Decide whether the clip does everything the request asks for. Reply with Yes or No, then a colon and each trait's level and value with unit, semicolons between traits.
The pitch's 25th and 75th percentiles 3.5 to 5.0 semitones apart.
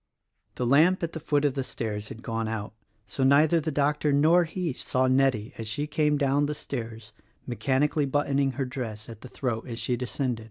Yes: average, 3.9 semitones